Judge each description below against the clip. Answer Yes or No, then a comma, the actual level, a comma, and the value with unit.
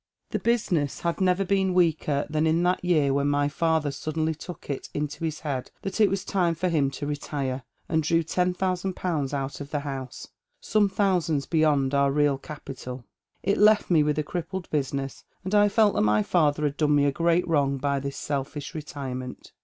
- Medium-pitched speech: Yes, medium, 155 Hz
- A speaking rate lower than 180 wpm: No, average, 200 wpm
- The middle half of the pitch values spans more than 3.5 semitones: Yes, average, 4.1 semitones